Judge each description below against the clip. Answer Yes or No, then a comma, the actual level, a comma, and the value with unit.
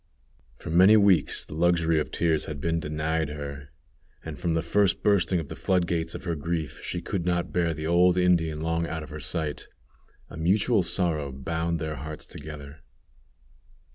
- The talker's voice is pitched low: Yes, very low, 80 Hz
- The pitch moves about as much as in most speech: No, narrow, 2.2 semitones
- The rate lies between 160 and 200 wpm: Yes, average, 180 wpm